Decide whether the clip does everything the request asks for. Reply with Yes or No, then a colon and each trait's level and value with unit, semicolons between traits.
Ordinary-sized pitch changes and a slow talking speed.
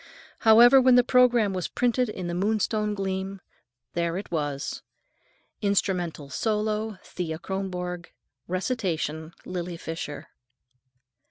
Yes: average, 4.0 semitones; slow, 105 wpm